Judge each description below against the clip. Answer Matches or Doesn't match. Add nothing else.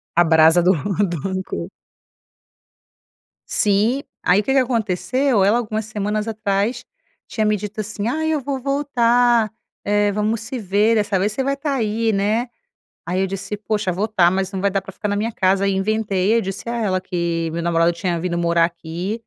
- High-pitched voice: Matches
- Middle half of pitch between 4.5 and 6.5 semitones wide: Doesn't match